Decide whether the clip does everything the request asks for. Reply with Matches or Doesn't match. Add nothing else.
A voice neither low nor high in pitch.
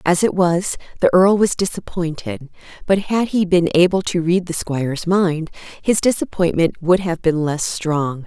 Matches